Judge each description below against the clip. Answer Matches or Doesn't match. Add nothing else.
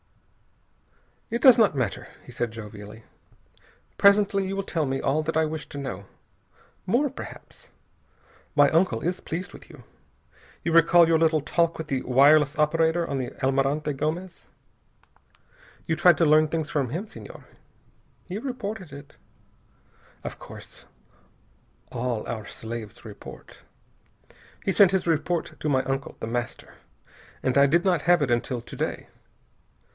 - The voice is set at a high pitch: Doesn't match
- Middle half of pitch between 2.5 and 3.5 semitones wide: Doesn't match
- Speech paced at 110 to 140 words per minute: Doesn't match